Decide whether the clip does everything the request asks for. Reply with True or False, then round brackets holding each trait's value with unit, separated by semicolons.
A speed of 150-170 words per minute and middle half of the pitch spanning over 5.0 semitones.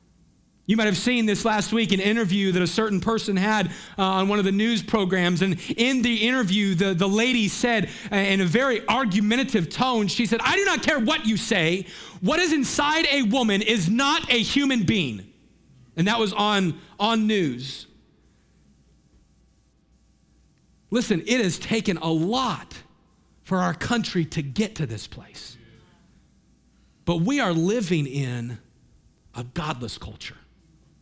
False (160 wpm; 4.7 semitones)